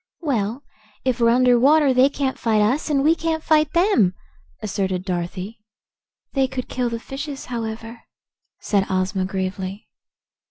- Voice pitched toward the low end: No, high, 235 Hz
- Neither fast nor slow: Yes, average, 145 wpm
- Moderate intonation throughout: No, wide, 5.7 semitones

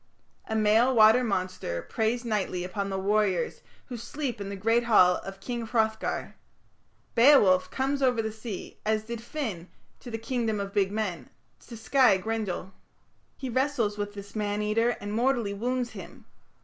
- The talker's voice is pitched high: Yes, high, 220 Hz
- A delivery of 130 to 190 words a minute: Yes, average, 160 wpm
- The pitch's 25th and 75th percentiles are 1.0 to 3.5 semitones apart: Yes, average, 3.0 semitones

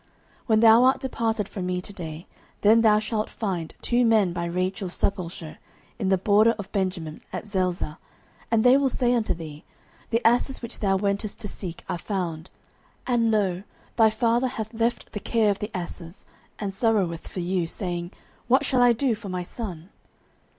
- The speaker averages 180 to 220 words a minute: Yes, average, 185 wpm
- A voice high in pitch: Yes, high, 205 Hz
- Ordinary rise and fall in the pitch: Yes, average, 4.0 semitones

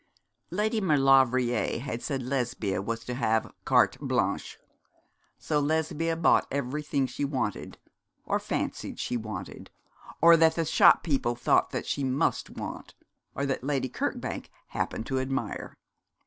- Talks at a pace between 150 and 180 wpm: No, slow, 135 wpm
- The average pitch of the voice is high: No, low, 135 Hz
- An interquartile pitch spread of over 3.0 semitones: Yes, average, 3.6 semitones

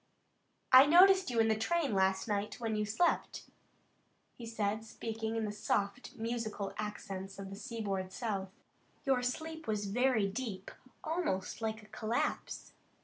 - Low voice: No, high, 220 Hz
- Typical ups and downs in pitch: Yes, average, 3.5 semitones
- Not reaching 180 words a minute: Yes, average, 145 wpm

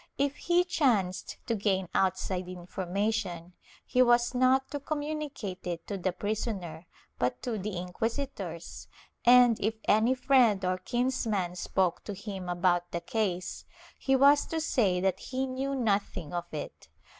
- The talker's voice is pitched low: No, high, 205 Hz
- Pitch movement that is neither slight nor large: No, wide, 5.8 semitones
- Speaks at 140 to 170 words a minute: Yes, average, 145 wpm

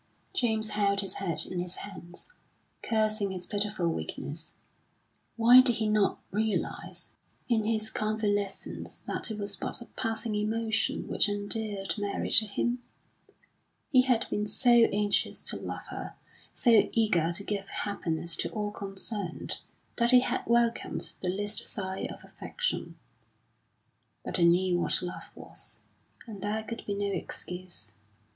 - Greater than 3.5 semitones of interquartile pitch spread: No, narrow, 2.4 semitones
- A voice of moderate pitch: No, high, 205 Hz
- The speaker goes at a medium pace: Yes, average, 145 wpm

